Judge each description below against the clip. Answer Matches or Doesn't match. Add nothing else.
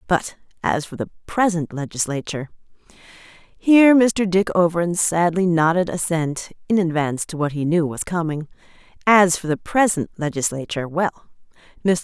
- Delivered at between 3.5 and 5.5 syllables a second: Matches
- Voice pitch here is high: Doesn't match